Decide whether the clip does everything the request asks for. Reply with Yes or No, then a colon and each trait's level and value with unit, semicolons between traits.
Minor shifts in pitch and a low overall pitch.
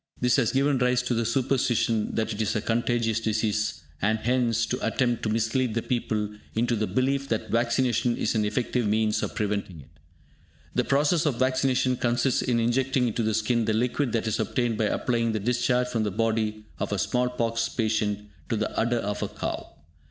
Yes: narrow, 2.3 semitones; low, 115 Hz